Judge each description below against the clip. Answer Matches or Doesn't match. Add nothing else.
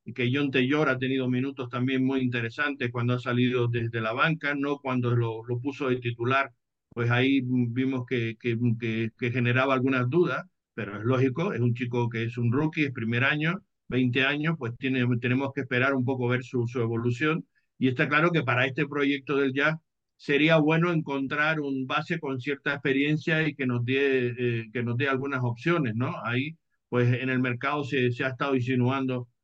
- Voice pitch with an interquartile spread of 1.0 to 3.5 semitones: Matches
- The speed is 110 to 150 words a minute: Doesn't match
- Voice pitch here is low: Matches